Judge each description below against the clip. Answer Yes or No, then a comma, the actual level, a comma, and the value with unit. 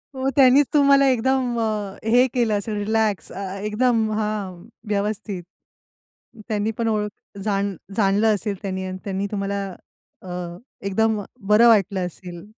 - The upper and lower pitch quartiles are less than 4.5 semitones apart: Yes, narrow, 2.4 semitones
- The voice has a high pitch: Yes, high, 210 Hz